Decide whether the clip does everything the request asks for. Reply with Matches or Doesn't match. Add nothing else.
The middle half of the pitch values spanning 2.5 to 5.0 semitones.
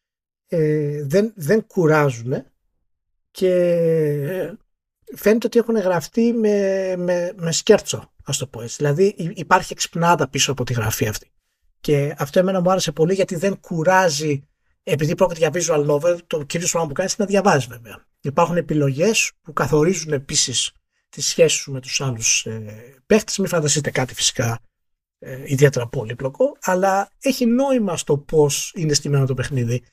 Doesn't match